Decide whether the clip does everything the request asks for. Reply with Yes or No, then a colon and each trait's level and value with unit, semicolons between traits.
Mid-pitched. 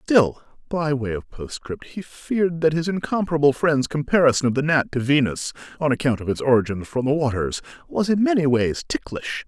Yes: medium, 145 Hz